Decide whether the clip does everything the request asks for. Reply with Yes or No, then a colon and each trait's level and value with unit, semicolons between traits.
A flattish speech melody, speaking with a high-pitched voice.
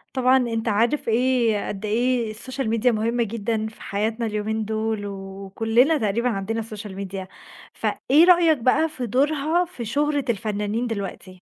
No: average, 3.3 semitones; high, 225 Hz